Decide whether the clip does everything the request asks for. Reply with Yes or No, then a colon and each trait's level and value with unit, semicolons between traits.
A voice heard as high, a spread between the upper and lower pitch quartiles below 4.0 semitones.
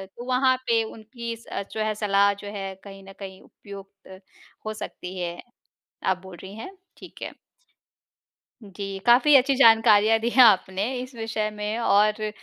Yes: high, 215 Hz; average, 2.9 semitones